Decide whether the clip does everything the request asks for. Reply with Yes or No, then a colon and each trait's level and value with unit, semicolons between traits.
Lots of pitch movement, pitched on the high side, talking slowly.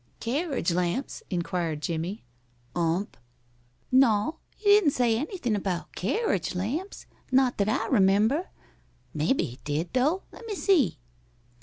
Yes: wide, 8.4 semitones; high, 220 Hz; slow, 120 wpm